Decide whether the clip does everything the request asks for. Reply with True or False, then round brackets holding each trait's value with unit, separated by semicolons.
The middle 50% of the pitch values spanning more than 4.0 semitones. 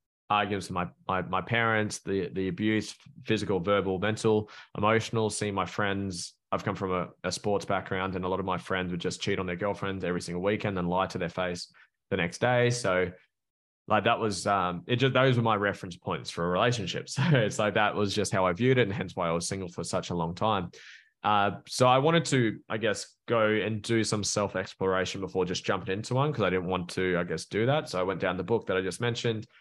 False (2.8 semitones)